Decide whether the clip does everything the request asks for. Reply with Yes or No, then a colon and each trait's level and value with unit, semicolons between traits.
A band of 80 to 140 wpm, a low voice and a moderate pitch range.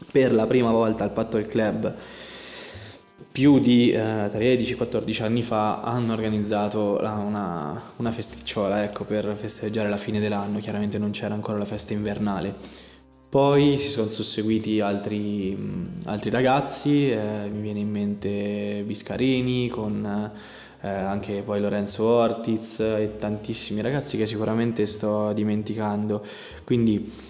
No: average, 135 wpm; low, 105 Hz; narrow, 1.6 semitones